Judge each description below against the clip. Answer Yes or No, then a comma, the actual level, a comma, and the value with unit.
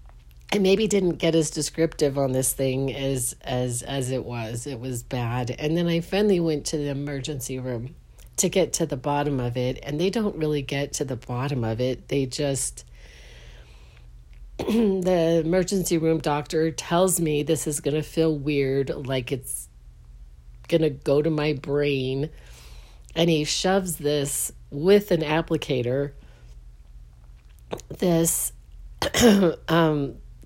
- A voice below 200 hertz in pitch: Yes, medium, 140 Hz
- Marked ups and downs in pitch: No, average, 4.8 semitones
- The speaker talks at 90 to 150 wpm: Yes, average, 140 wpm